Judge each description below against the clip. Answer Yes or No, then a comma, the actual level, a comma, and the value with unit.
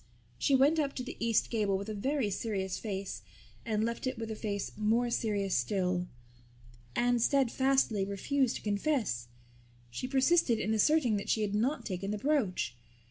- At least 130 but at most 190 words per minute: Yes, average, 170 wpm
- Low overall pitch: No, high, 220 Hz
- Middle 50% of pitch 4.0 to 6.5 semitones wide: Yes, average, 4.6 semitones